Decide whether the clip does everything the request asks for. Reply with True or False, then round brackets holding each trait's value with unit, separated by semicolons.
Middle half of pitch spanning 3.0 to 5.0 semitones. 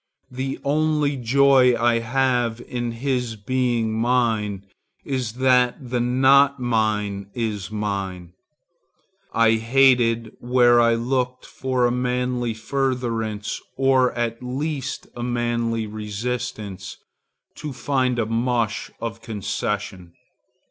False (2.4 semitones)